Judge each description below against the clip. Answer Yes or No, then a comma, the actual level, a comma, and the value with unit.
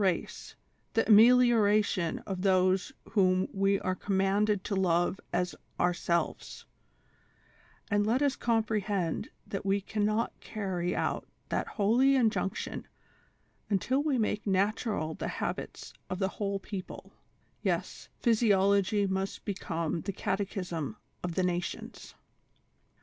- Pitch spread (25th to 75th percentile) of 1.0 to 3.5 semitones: Yes, narrow, 2.5 semitones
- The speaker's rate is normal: No, slow, 120 wpm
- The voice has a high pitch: Yes, high, 195 Hz